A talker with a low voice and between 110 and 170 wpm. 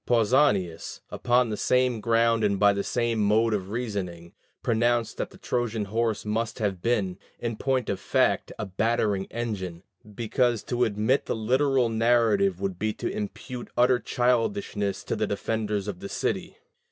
Yes: low, 110 Hz; average, 160 wpm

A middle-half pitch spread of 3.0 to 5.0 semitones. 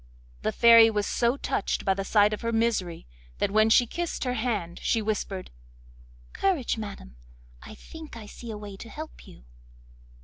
No: narrow, 2.6 semitones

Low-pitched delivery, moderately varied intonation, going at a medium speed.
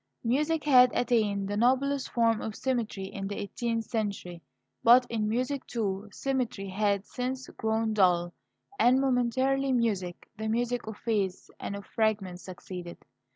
No: high, 225 Hz; average, 3.8 semitones; average, 145 wpm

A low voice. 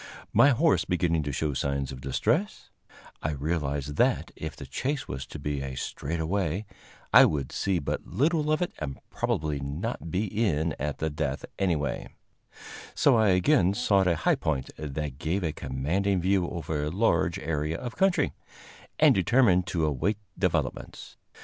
Yes: very low, 80 Hz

